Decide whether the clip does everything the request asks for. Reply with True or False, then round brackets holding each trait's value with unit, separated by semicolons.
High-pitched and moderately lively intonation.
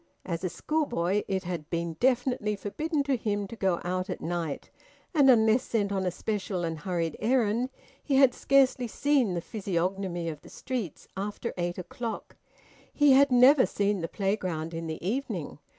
False (200 Hz; 6.1 semitones)